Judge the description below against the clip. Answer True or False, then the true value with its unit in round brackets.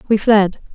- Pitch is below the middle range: False (205 Hz)